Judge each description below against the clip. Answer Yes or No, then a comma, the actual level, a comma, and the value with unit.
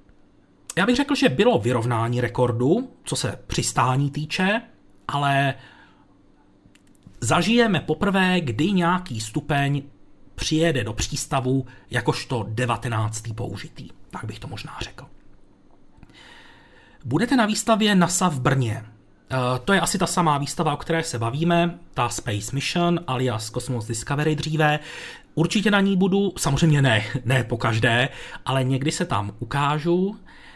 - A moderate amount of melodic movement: No, wide, 5.9 semitones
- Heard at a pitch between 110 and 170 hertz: Yes, medium, 140 Hz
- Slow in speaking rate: No, average, 130 wpm